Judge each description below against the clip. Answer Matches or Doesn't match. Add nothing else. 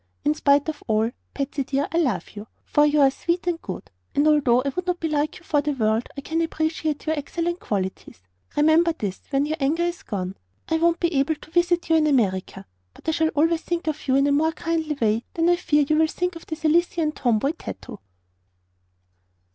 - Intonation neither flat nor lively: Matches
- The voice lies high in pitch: Matches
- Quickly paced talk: Matches